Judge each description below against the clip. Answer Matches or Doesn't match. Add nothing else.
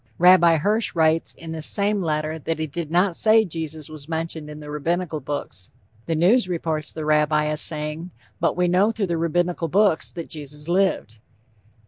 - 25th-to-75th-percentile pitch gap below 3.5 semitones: Matches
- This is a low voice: Doesn't match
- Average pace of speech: Matches